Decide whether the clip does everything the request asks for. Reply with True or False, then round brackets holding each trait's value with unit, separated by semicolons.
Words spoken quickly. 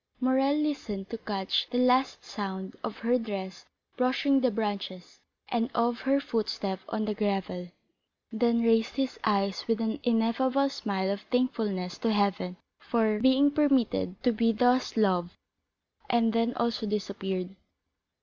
False (140 wpm)